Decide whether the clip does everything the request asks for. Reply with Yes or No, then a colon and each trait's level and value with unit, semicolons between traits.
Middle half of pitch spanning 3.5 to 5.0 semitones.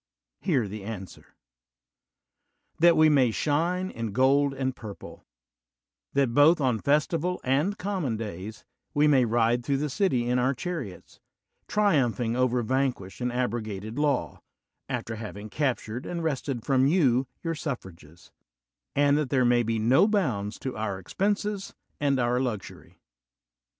Yes: average, 4.7 semitones